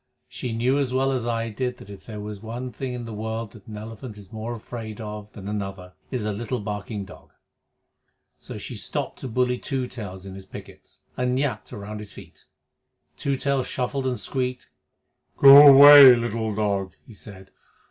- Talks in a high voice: No, low, 115 Hz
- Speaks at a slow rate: No, average, 190 wpm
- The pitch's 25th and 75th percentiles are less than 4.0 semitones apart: Yes, average, 3.3 semitones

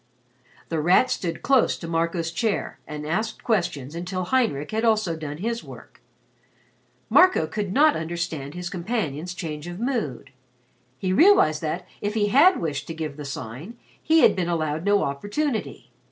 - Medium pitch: Yes, medium, 175 Hz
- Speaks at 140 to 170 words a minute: Yes, average, 160 wpm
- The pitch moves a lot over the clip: Yes, wide, 5.8 semitones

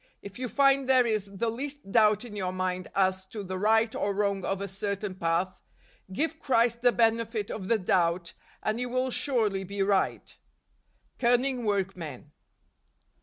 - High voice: Yes, high, 210 Hz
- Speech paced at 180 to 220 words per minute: No, average, 165 wpm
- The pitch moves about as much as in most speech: Yes, average, 3.9 semitones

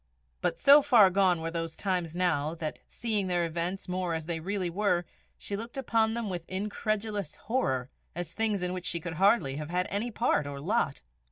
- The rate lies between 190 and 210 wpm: Yes, average, 195 wpm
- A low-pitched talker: No, medium, 180 Hz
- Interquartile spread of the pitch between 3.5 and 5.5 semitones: Yes, average, 4.0 semitones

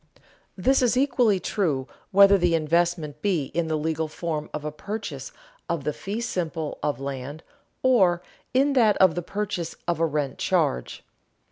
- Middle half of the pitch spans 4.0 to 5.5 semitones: Yes, average, 4.9 semitones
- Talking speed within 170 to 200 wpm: No, average, 160 wpm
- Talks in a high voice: No, medium, 170 Hz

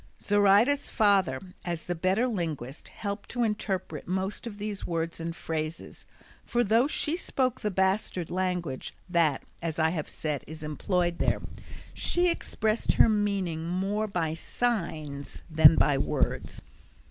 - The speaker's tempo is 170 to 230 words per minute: No, average, 140 wpm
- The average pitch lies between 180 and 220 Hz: Yes, medium, 185 Hz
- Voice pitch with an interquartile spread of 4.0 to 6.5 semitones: Yes, average, 4.6 semitones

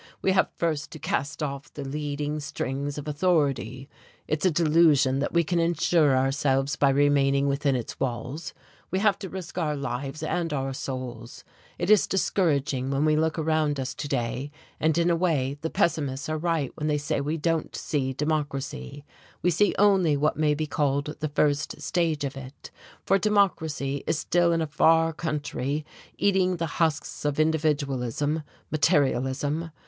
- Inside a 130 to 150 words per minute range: No, average, 170 wpm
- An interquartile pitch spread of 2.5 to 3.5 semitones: Yes, average, 2.9 semitones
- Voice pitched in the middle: Yes, medium, 150 Hz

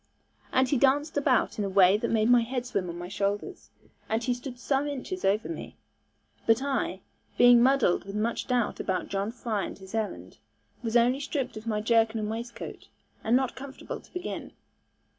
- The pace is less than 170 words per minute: No, average, 190 wpm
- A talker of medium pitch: No, high, 235 Hz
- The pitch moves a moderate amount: Yes, average, 3.9 semitones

